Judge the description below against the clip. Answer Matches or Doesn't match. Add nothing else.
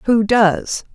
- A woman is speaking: Matches